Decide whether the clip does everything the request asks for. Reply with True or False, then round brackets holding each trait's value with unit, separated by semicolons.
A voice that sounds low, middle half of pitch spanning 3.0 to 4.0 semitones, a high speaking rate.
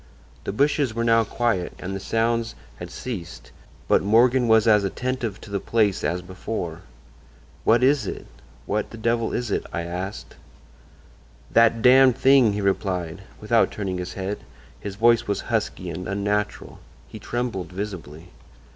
False (105 Hz; 3.5 semitones; 155 wpm)